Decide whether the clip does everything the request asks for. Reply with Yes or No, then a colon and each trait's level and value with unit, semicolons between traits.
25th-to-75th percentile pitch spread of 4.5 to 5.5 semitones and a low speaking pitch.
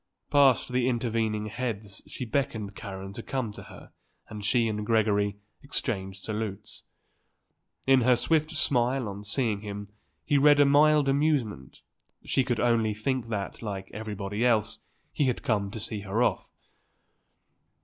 No: average, 3.9 semitones; low, 115 Hz